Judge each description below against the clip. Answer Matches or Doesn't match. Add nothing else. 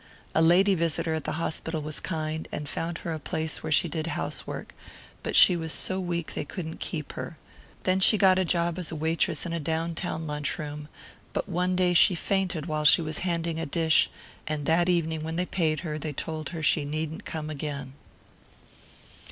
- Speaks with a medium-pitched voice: Matches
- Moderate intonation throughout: Doesn't match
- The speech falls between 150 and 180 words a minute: Doesn't match